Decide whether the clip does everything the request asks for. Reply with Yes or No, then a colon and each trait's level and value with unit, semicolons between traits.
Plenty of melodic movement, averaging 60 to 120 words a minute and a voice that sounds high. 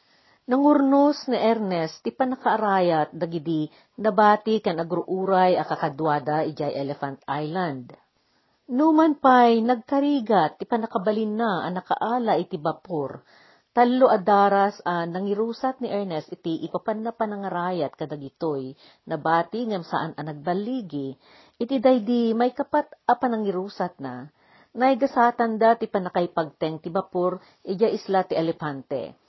Yes: wide, 6.3 semitones; average, 115 wpm; high, 195 Hz